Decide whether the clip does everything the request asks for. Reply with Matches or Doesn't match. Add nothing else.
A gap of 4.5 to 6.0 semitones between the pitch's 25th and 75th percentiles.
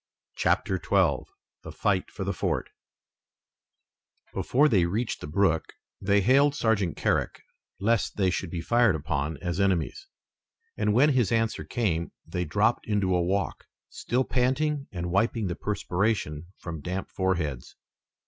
Matches